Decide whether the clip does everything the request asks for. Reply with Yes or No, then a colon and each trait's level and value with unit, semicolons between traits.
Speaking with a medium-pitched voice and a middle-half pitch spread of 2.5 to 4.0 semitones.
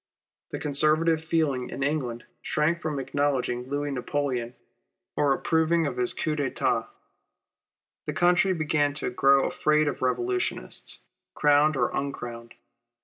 Yes: medium, 145 Hz; average, 2.9 semitones